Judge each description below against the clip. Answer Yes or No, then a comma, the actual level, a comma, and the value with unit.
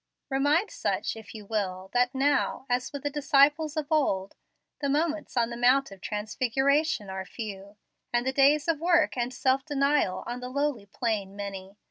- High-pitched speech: Yes, very high, 255 Hz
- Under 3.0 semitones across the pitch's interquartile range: No, wide, 5.4 semitones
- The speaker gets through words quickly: No, average, 175 wpm